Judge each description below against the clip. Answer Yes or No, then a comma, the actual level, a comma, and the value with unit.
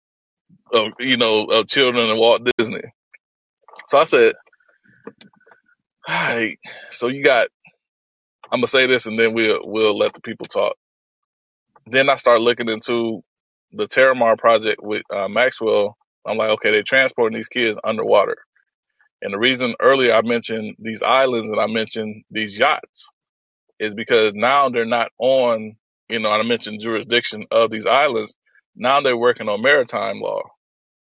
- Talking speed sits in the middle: Yes, average, 155 wpm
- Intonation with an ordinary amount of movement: Yes, average, 3.4 semitones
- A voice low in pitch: Yes, low, 115 Hz